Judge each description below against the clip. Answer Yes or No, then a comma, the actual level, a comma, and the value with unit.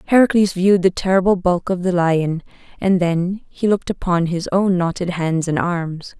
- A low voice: No, medium, 180 Hz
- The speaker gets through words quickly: No, average, 185 wpm